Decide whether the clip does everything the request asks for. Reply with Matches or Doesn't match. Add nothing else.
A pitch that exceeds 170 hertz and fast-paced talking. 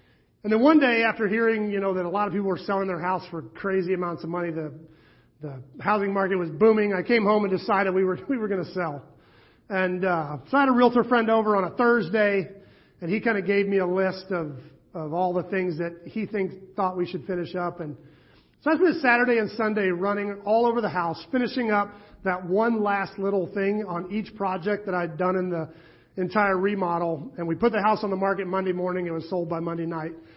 Matches